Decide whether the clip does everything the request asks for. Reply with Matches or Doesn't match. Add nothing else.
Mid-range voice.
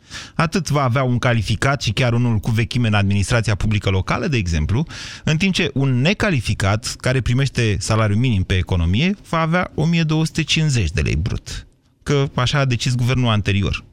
Doesn't match